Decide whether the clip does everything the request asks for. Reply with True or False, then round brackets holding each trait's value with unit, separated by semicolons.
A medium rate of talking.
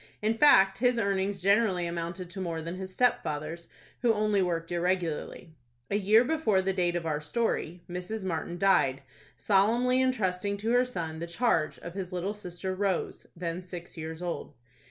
True (170 wpm)